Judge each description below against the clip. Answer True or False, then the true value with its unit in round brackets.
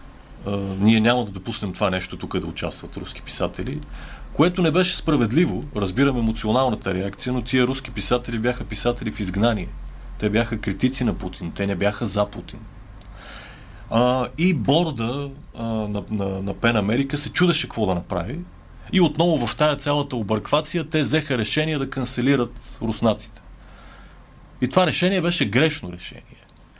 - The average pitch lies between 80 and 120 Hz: True (115 Hz)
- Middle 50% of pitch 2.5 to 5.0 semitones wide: False (5.4 semitones)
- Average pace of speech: True (145 wpm)